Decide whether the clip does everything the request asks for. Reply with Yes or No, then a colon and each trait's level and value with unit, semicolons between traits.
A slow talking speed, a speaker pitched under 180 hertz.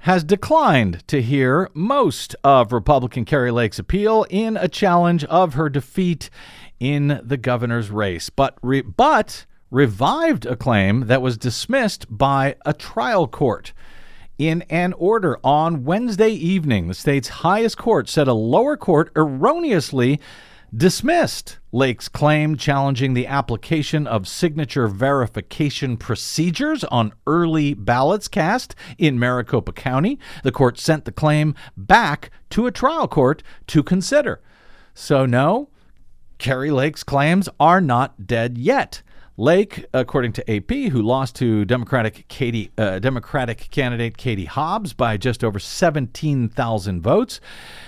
Yes: slow, 130 wpm; low, 135 Hz